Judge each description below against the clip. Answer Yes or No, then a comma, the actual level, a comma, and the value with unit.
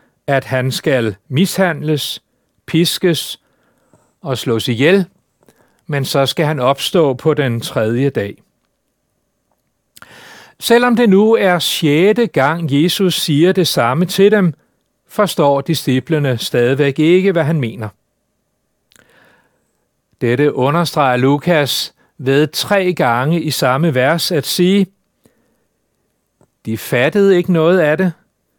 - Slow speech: Yes, slow, 110 wpm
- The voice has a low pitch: No, medium, 155 Hz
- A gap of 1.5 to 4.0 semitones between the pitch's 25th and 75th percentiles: No, average, 5.3 semitones